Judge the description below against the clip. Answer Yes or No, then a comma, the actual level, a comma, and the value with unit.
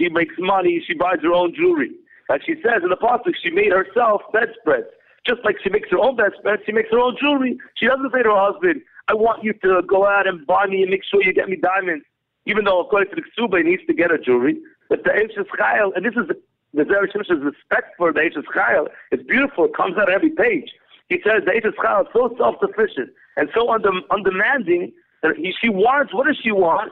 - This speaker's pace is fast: Yes, fast, 240 wpm